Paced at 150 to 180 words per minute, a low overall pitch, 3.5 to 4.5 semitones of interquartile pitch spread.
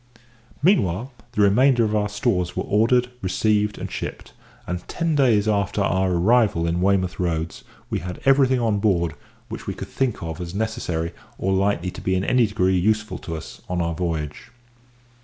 Yes: average, 175 wpm; low, 100 Hz; average, 3.9 semitones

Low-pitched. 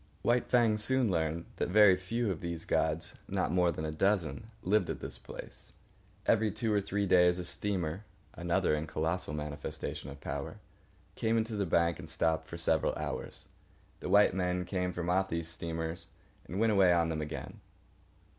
Yes: very low, 90 Hz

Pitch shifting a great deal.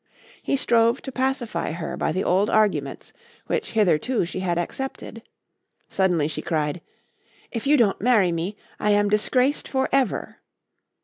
Yes: wide, 6.1 semitones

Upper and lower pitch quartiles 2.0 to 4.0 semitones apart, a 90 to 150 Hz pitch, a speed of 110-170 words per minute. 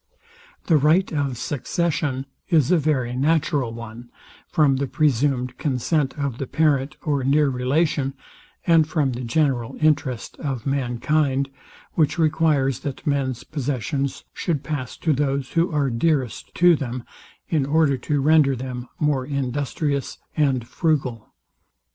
Yes: average, 3.0 semitones; medium, 140 Hz; slow, 135 wpm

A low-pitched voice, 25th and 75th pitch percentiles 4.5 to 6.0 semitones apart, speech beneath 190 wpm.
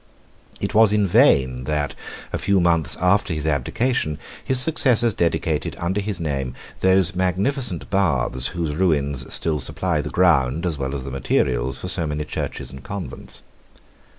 Yes: very low, 80 Hz; average, 5.1 semitones; average, 155 wpm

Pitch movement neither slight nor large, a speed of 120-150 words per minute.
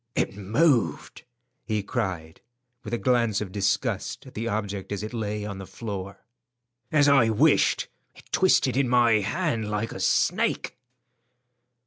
Yes: average, 3.5 semitones; average, 145 wpm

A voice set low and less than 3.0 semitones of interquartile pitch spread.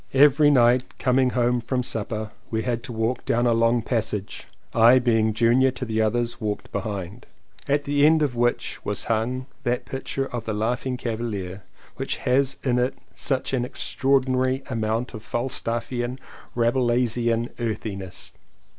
Yes: low, 120 Hz; narrow, 2.4 semitones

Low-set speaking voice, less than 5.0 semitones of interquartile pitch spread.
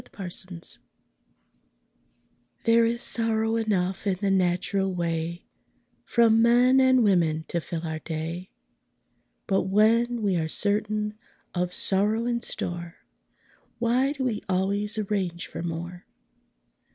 No: high, 200 Hz; average, 4.4 semitones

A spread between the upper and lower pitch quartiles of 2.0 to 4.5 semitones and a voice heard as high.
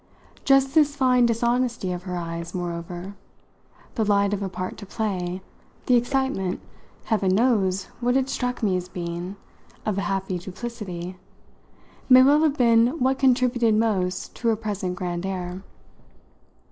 No: average, 5.2 semitones; high, 205 Hz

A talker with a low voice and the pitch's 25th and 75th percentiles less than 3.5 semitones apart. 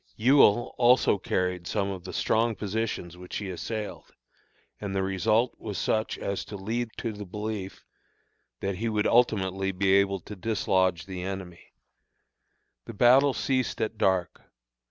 Yes: low, 100 Hz; average, 2.9 semitones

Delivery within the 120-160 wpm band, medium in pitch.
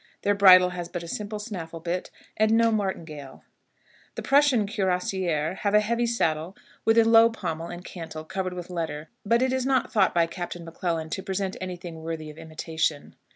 No: average, 190 wpm; medium, 180 Hz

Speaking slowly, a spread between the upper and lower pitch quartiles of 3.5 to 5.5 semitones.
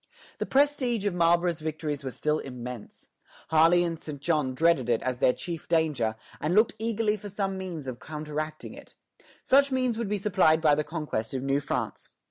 No: average, 185 wpm; average, 5.1 semitones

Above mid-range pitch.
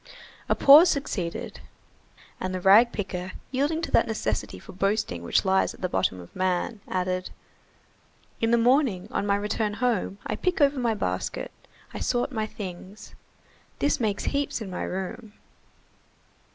Yes: high, 205 Hz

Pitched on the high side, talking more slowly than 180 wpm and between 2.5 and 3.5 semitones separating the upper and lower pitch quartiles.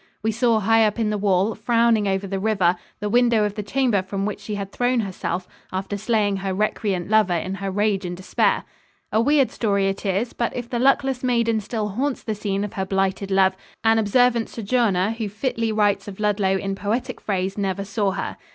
No: high, 210 Hz; fast, 205 wpm; average, 2.8 semitones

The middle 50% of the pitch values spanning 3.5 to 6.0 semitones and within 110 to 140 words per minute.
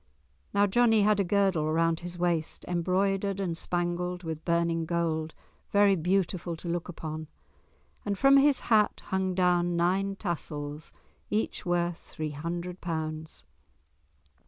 No: average, 2.9 semitones; slow, 135 wpm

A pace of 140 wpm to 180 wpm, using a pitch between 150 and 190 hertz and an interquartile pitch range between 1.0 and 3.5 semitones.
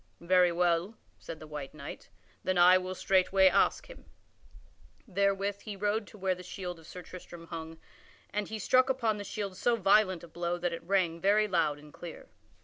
No: average, 190 wpm; medium, 185 Hz; average, 2.9 semitones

